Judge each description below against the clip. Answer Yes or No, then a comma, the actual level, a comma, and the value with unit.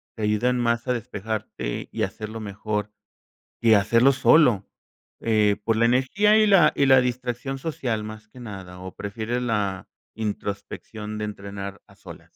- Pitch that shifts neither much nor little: Yes, average, 3.1 semitones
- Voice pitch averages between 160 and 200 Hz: No, low, 110 Hz